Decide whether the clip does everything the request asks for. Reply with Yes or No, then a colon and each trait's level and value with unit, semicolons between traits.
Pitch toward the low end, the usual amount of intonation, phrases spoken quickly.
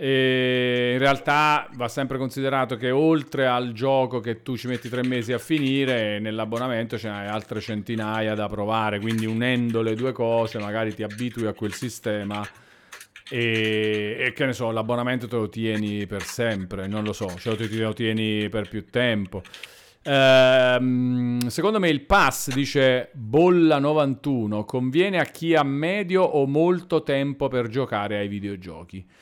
No: low, 120 Hz; average, 3.8 semitones; average, 160 wpm